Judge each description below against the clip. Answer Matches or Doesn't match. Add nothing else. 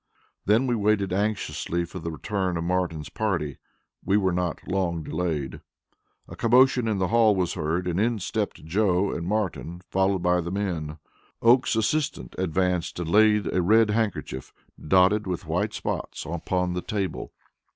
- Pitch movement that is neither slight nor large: Matches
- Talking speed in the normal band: Matches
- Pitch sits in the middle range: Doesn't match